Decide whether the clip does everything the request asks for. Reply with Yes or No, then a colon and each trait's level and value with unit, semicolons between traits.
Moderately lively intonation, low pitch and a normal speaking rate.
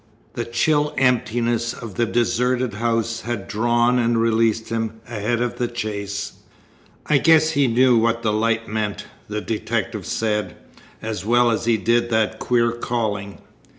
No: narrow, 1.7 semitones; low, 115 Hz; average, 150 wpm